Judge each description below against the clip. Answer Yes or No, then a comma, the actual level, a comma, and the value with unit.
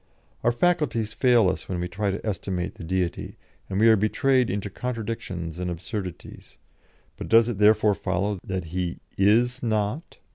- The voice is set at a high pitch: No, low, 105 Hz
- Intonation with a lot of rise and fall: No, average, 3.8 semitones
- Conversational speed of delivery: Yes, average, 160 wpm